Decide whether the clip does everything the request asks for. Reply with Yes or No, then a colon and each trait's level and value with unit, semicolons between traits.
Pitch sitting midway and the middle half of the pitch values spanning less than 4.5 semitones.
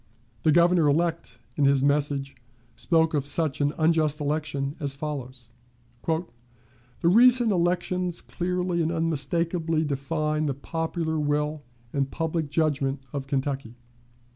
Yes: medium, 155 Hz; average, 2.8 semitones